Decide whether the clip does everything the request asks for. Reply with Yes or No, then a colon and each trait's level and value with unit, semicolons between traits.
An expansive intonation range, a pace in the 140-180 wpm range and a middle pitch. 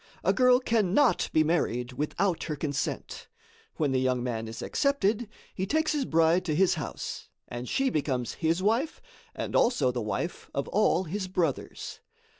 Yes: wide, 8.0 semitones; average, 165 wpm; medium, 165 Hz